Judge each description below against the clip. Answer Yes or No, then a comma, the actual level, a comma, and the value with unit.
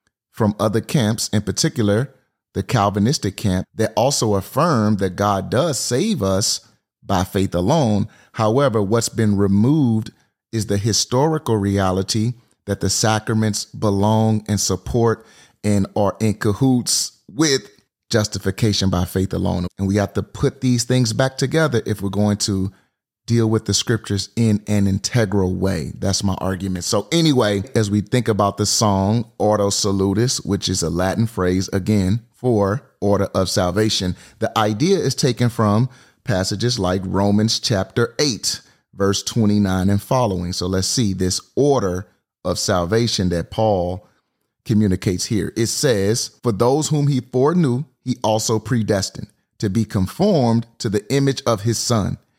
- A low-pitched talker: Yes, low, 105 Hz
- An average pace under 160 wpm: Yes, average, 150 wpm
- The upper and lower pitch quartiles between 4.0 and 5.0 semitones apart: No, average, 3.1 semitones